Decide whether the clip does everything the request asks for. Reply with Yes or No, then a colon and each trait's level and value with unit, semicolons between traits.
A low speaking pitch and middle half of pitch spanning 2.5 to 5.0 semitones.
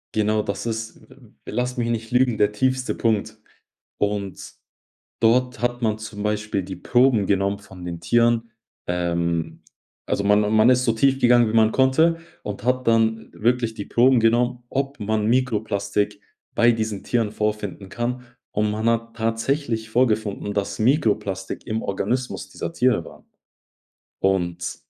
Yes: low, 110 Hz; average, 2.9 semitones